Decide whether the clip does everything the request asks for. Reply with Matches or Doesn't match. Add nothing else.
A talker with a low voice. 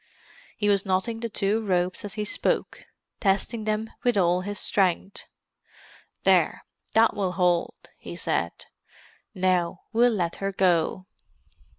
Doesn't match